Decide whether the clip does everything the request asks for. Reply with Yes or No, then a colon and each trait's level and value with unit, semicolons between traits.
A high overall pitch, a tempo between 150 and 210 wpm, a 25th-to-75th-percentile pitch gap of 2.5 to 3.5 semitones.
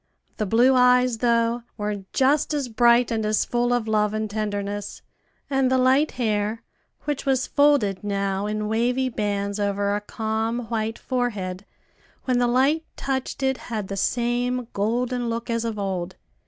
Yes: high, 230 Hz; average, 160 wpm; average, 3.2 semitones